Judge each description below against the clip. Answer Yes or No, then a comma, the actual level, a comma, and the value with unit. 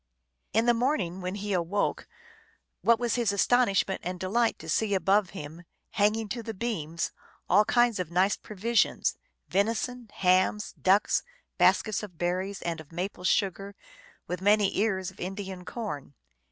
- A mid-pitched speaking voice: No, high, 200 Hz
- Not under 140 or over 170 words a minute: Yes, average, 155 wpm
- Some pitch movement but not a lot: Yes, average, 3.4 semitones